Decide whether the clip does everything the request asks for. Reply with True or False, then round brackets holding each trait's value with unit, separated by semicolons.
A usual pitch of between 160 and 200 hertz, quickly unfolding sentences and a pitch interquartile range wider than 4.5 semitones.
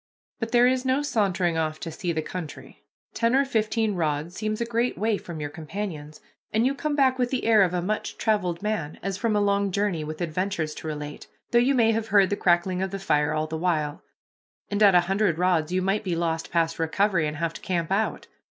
True (190 Hz; 230 wpm; 4.9 semitones)